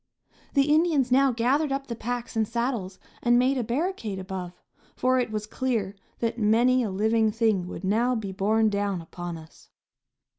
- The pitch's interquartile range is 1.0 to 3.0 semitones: No, average, 3.9 semitones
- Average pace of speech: Yes, average, 175 wpm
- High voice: Yes, high, 230 Hz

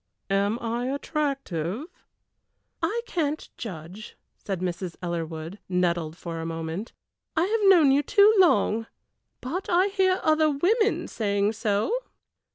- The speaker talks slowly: Yes, slow, 125 wpm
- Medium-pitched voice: No, high, 225 Hz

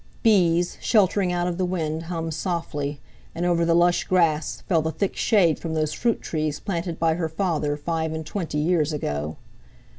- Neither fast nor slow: Yes, average, 180 wpm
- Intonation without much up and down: Yes, narrow, 2.3 semitones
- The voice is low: No, medium, 165 Hz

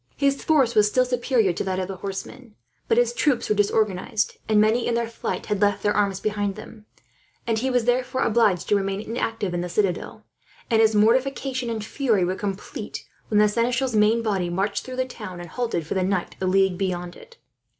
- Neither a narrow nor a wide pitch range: Yes, average, 3.9 semitones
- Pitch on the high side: Yes, high, 215 Hz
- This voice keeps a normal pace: No, fast, 210 wpm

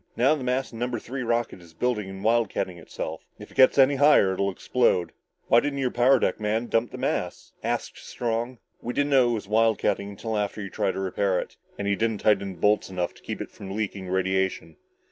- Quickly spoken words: Yes, fast, 225 wpm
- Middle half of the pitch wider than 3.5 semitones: Yes, average, 4.1 semitones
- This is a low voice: Yes, low, 110 Hz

